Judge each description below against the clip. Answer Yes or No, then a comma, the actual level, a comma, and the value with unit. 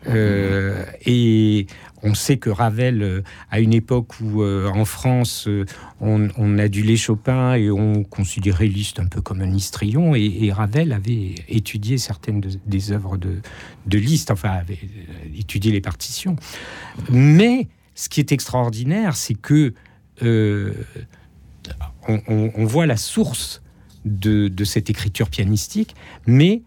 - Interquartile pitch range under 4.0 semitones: Yes, average, 3.3 semitones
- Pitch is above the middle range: No, low, 110 Hz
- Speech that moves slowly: Yes, slow, 140 wpm